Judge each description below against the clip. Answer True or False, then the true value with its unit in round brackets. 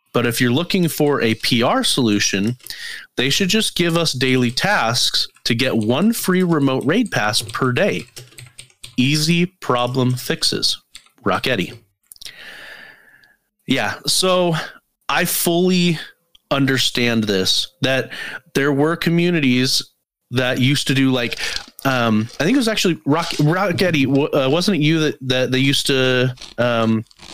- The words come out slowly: True (130 wpm)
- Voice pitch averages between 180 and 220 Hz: False (135 Hz)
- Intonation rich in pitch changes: True (5.8 semitones)